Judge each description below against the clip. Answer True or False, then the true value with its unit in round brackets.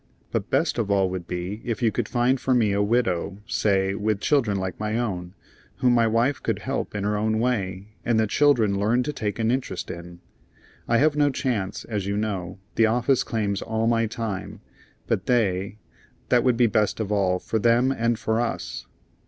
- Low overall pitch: True (110 Hz)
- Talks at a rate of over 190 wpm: True (200 wpm)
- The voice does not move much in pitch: False (3.2 semitones)